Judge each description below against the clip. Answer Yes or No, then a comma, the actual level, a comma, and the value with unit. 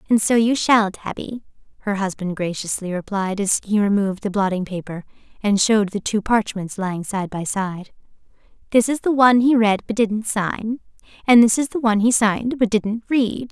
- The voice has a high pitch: Yes, high, 210 Hz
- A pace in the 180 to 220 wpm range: Yes, average, 190 wpm